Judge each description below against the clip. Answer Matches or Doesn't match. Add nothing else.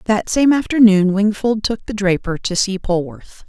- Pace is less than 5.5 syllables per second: Matches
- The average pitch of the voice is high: Matches